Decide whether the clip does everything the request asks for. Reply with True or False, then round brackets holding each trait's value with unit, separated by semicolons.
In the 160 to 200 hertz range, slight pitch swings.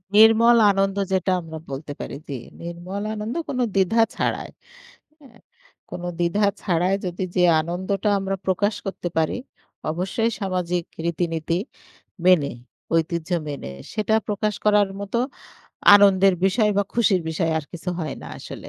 False (190 Hz; 3.3 semitones)